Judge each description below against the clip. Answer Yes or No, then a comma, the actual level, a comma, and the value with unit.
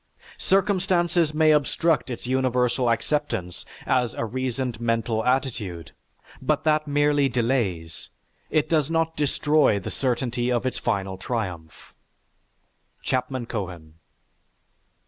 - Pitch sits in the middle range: No, low, 125 Hz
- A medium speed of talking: No, slow, 105 wpm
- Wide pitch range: No, average, 4.7 semitones